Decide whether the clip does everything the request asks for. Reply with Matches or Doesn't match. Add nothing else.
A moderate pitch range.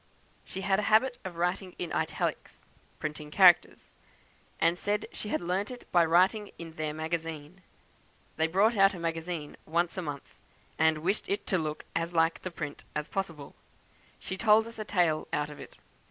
Matches